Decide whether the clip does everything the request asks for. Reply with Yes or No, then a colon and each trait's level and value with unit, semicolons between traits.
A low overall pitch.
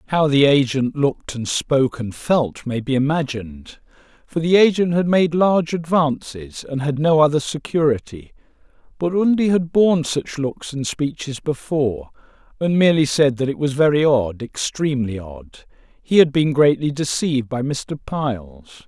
No: medium, 145 Hz